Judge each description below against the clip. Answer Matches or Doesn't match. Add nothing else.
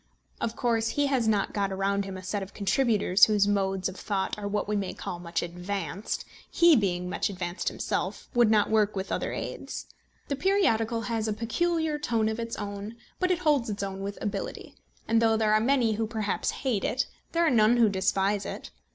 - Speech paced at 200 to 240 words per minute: Matches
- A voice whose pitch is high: Matches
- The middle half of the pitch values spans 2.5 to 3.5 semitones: Matches